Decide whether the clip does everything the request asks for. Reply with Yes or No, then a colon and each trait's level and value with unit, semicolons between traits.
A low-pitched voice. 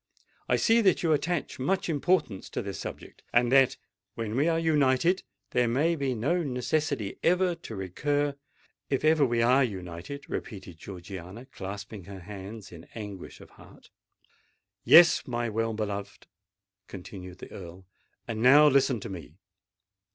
Yes: low, 120 Hz